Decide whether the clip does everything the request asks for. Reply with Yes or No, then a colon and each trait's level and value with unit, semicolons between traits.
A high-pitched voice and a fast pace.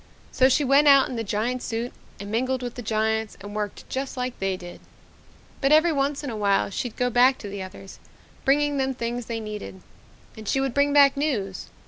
Yes: high, 245 Hz; fast, 210 wpm